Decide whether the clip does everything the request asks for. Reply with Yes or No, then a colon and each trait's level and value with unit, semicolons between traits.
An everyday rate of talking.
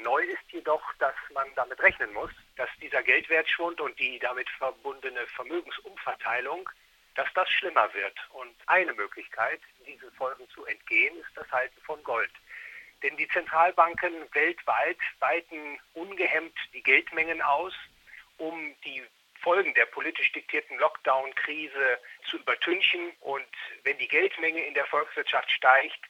Yes: average, 135 wpm